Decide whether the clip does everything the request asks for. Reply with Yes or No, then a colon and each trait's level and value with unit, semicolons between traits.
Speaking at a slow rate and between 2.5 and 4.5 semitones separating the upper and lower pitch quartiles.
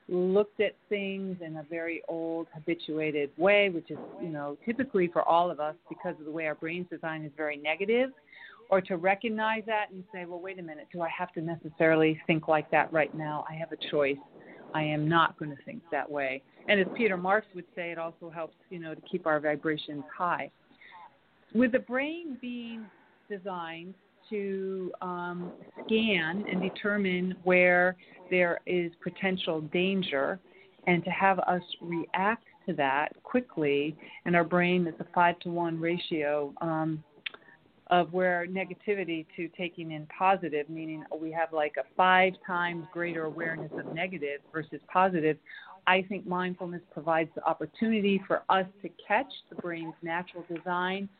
No: average, 170 wpm; average, 3.0 semitones